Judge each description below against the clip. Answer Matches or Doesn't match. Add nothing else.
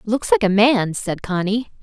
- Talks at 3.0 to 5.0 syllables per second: Matches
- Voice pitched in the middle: Doesn't match